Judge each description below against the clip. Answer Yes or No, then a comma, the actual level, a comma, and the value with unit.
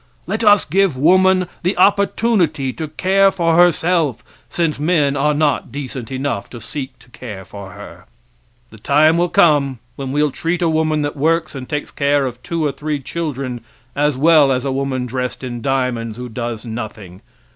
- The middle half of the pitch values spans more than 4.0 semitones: Yes, average, 4.6 semitones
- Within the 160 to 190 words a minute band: Yes, average, 180 wpm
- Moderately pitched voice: Yes, medium, 145 Hz